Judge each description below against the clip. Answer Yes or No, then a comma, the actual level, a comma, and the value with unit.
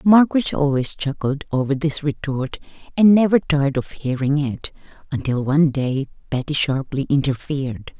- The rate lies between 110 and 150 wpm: Yes, slow, 135 wpm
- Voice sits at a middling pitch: Yes, medium, 145 Hz